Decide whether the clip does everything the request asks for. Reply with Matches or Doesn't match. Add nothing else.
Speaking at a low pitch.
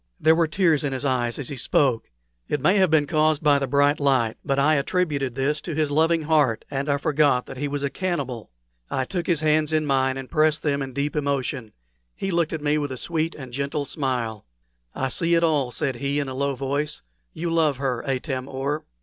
Doesn't match